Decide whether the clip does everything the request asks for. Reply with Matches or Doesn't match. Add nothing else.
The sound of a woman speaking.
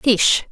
Matches